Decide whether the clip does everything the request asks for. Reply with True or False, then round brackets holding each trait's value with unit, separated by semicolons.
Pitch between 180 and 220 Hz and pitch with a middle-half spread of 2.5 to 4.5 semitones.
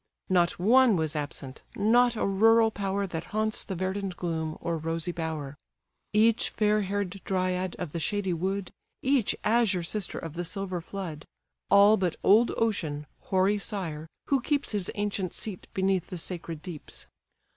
True (190 Hz; 3.7 semitones)